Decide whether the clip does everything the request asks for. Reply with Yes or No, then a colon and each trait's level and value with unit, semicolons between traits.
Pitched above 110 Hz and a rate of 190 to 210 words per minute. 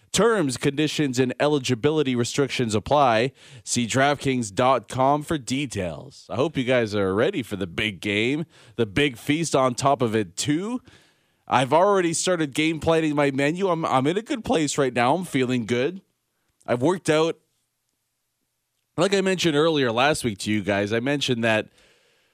No: low, 135 Hz; average, 165 wpm